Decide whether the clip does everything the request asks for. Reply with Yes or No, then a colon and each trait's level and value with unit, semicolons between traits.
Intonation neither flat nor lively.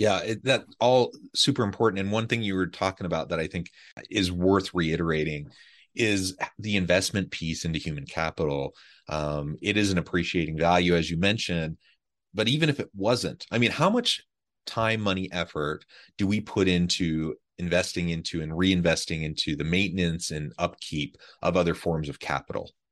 Yes: average, 3.5 semitones